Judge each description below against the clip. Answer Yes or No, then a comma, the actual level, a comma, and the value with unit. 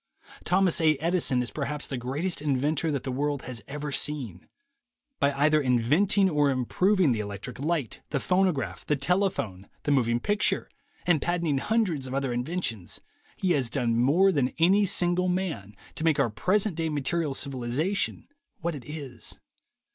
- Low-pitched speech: No, medium, 145 Hz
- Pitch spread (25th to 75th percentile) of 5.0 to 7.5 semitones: Yes, wide, 5.4 semitones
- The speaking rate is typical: Yes, average, 160 wpm